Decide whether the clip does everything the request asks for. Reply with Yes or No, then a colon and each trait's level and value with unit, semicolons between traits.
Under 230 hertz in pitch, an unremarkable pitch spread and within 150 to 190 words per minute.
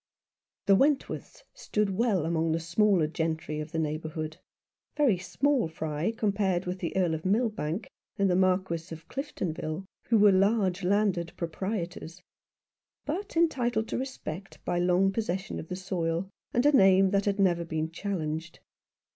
Yes: medium, 185 Hz; average, 4.2 semitones; average, 155 wpm